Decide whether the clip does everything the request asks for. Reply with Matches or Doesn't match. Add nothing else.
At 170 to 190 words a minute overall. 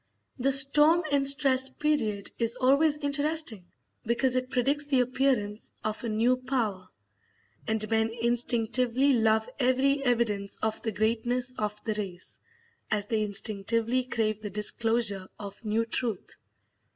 Doesn't match